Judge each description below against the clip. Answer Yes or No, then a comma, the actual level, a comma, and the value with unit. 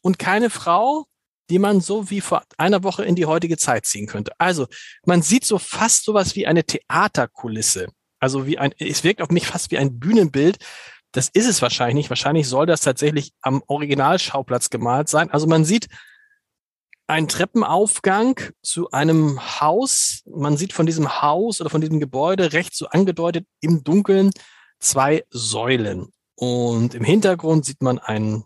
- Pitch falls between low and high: Yes, medium, 160 Hz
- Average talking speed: Yes, average, 165 wpm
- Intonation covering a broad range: Yes, wide, 5.7 semitones